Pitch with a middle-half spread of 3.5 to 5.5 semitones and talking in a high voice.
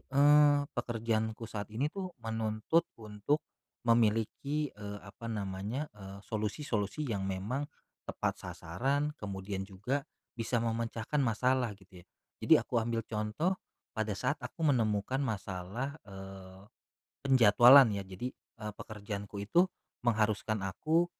No: average, 4.5 semitones; low, 110 Hz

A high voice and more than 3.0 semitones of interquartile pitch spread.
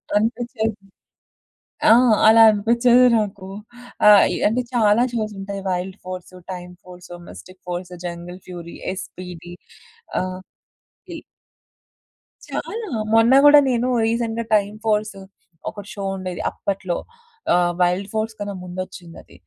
Yes: high, 200 Hz; average, 3.6 semitones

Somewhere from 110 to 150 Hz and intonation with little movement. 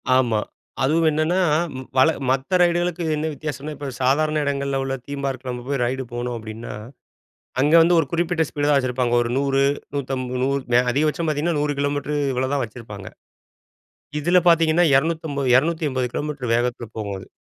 No: medium, 140 Hz; average, 3.4 semitones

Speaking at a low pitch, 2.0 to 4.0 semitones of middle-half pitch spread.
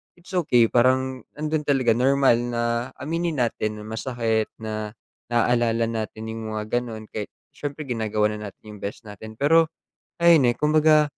No: low, 120 Hz; average, 4.6 semitones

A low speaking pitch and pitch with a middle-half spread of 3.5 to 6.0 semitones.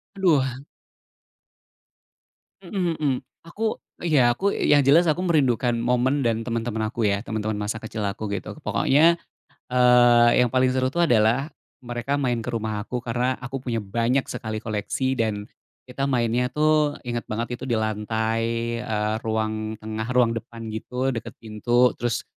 No: low, 120 Hz; average, 3.1 semitones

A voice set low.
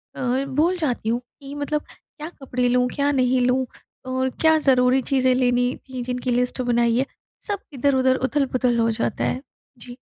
No: very high, 255 Hz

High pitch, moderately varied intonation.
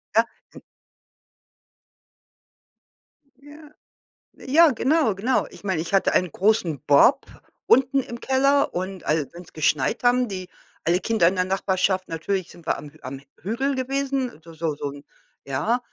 No: high, 195 Hz; wide, 7.6 semitones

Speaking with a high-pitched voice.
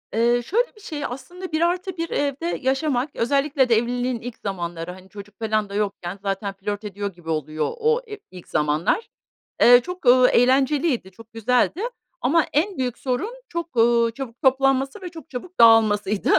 Yes: high, 245 Hz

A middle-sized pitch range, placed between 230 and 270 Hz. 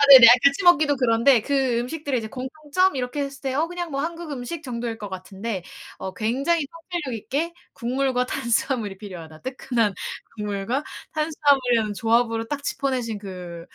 Yes: average, 4.3 semitones; very high, 255 Hz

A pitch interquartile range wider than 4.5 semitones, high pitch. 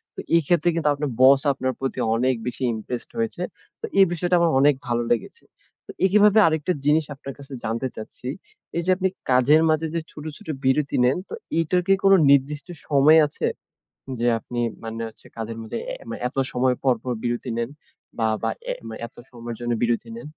No: average, 5.1 semitones; low, 135 Hz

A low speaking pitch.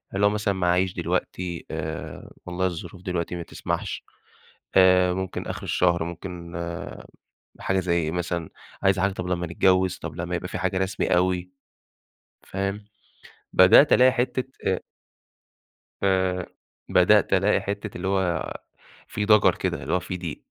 Yes: very low, 90 Hz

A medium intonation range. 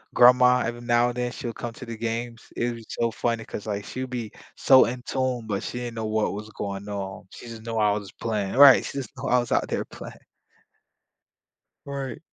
No: narrow, 2.3 semitones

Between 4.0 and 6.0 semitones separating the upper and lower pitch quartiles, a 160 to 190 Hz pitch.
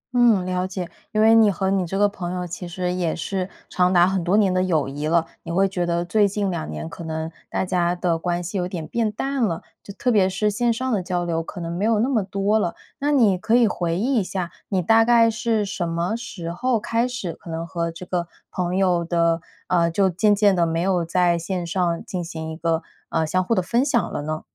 No: average, 3.5 semitones; medium, 185 Hz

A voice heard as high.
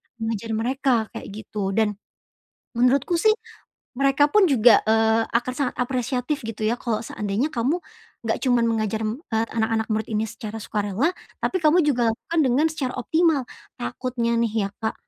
Yes: high, 235 Hz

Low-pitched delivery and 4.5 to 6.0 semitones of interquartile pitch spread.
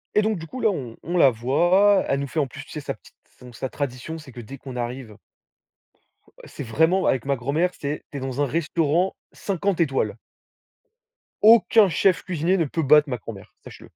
No: medium, 150 Hz; average, 5.2 semitones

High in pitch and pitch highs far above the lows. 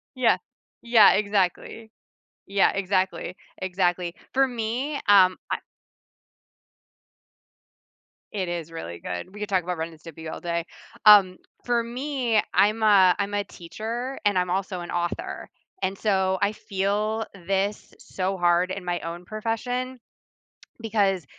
No: high, 195 Hz; average, 3.4 semitones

